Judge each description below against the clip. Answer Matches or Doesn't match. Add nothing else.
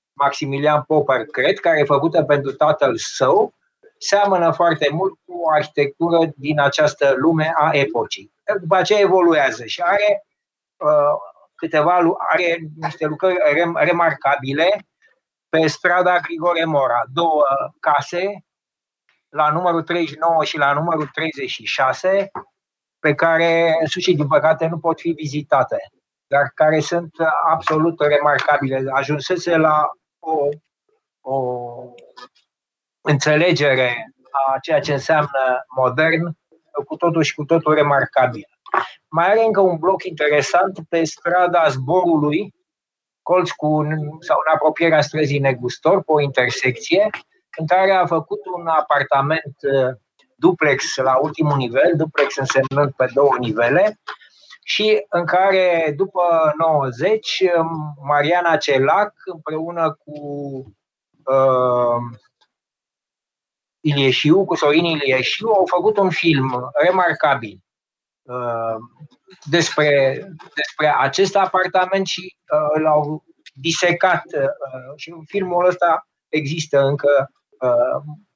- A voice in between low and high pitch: Matches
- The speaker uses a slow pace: Matches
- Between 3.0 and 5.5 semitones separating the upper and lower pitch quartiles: Matches